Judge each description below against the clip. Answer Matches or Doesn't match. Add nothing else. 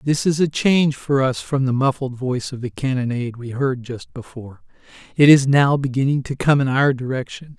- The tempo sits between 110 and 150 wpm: Doesn't match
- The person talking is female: Doesn't match